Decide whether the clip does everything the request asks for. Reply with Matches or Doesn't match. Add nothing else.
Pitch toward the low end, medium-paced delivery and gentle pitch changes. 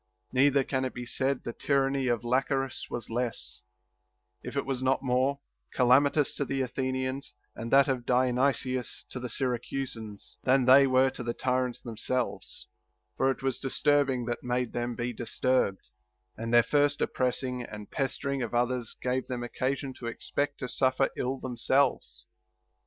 Matches